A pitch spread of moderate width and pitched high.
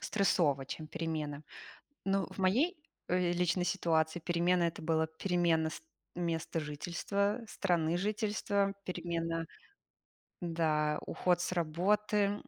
No: average, 3.4 semitones; medium, 175 Hz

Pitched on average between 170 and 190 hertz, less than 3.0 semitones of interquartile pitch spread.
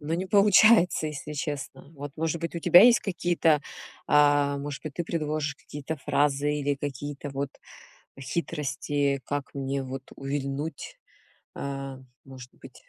No: medium, 145 Hz; narrow, 2.5 semitones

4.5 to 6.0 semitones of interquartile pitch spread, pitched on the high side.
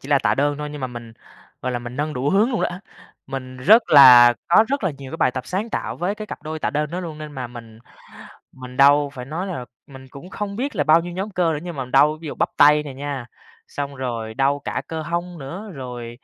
No: average, 4.9 semitones; medium, 145 Hz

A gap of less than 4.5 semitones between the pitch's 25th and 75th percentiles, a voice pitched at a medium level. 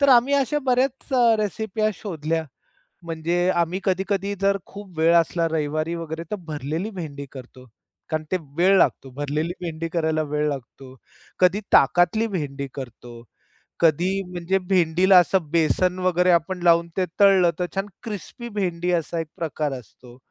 Yes: average, 3.6 semitones; medium, 170 Hz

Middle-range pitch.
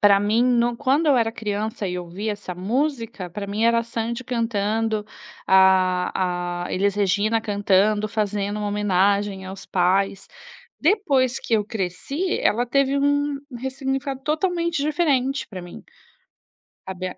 No: high, 215 Hz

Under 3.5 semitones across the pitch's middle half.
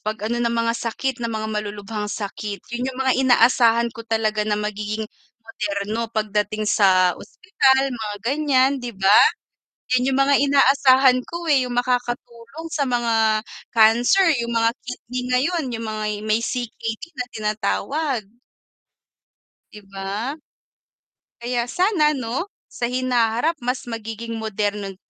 Yes: average, 3.1 semitones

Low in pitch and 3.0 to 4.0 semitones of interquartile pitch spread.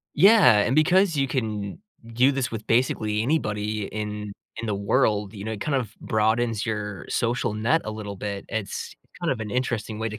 Yes: low, 110 Hz; average, 3.3 semitones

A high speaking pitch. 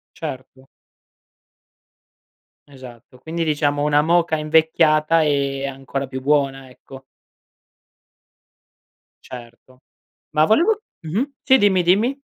No: medium, 150 Hz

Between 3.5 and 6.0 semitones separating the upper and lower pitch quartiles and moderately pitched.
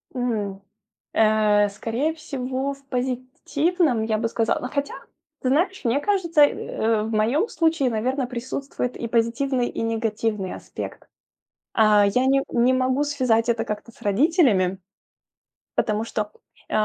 No: average, 4.0 semitones; high, 245 Hz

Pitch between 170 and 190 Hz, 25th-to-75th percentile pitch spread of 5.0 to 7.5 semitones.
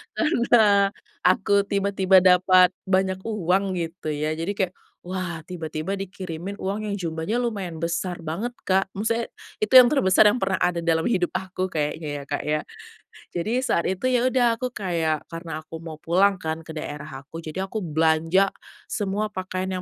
No: medium, 185 Hz; average, 3.4 semitones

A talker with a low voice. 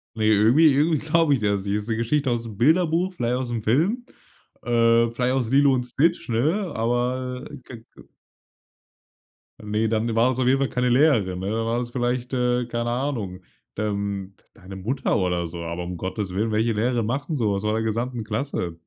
Yes: low, 120 Hz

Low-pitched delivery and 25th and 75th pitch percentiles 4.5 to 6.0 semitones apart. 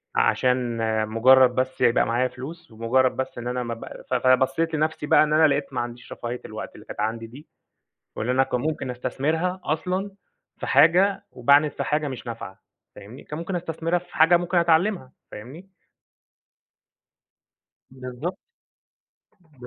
Yes: low, 130 Hz; average, 4.8 semitones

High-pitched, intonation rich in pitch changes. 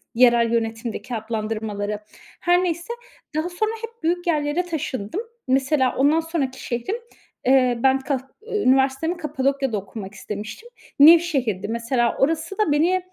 Yes: very high, 270 Hz; wide, 6.0 semitones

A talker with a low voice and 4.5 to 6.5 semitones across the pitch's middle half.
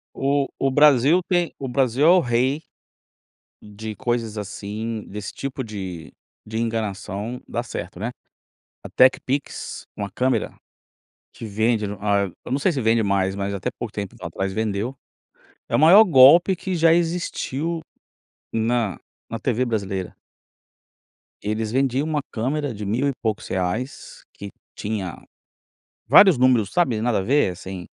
Yes: low, 115 Hz; average, 5.0 semitones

